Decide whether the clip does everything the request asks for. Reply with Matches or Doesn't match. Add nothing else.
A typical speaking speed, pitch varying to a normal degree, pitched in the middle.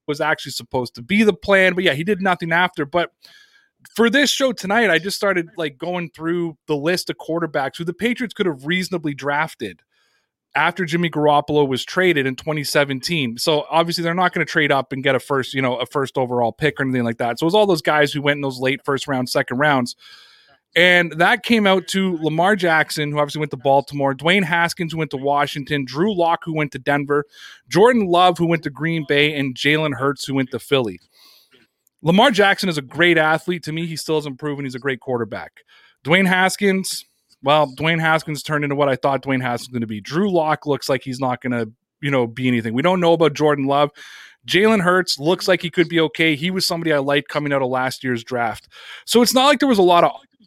Doesn't match